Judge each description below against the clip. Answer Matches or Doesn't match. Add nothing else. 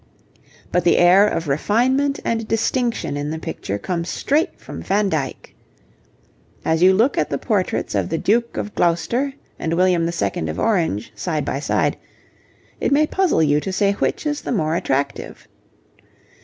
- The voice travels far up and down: Matches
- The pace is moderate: Matches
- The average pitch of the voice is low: Doesn't match